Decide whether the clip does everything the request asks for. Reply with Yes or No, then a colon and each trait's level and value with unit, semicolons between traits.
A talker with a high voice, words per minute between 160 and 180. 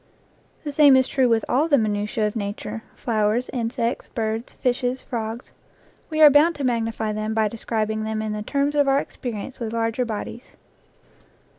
Yes: high, 230 Hz; average, 170 wpm